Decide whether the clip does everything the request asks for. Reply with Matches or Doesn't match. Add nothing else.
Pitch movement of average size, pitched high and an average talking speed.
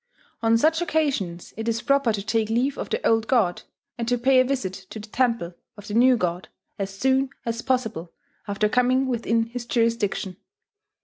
Matches